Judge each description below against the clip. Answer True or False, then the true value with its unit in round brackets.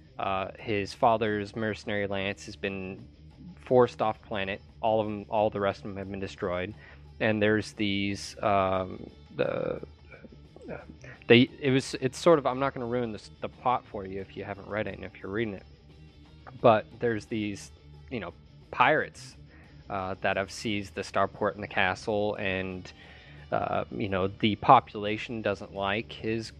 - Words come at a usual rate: True (175 wpm)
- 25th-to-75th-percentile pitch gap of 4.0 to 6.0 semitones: False (2.9 semitones)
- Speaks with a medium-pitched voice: False (100 Hz)